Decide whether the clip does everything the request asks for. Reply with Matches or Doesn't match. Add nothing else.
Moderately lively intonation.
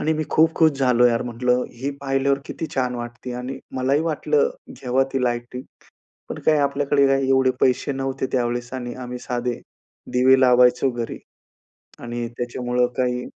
Doesn't match